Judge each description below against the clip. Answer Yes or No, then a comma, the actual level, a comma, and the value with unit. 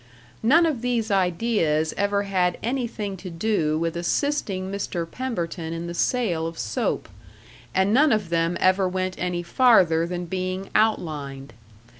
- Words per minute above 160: No, average, 145 wpm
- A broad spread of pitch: No, average, 4.6 semitones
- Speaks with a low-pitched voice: No, medium, 185 Hz